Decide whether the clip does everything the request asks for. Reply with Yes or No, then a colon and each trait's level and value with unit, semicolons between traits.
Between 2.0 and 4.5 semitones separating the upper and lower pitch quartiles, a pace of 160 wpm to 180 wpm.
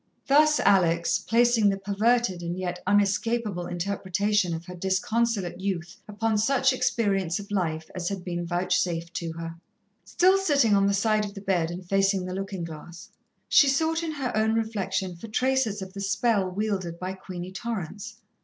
Yes: average, 3.8 semitones; average, 170 wpm